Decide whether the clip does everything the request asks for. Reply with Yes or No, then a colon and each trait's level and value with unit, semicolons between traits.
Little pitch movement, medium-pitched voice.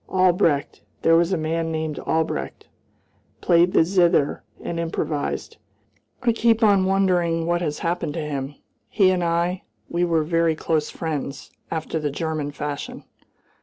Yes: narrow, 2.3 semitones; medium, 165 Hz